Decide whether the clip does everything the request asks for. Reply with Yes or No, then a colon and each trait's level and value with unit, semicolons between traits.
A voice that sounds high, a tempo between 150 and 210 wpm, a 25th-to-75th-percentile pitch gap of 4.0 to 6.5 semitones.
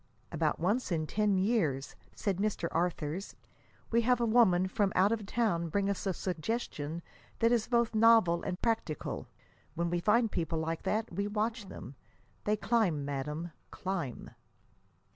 Yes: high, 195 Hz; average, 155 wpm; average, 4.9 semitones